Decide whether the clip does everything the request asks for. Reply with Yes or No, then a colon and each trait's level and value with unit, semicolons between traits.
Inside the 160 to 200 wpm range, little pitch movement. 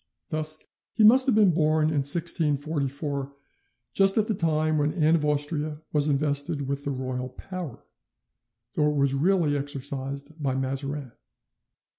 No: average, 145 wpm; narrow, 2.3 semitones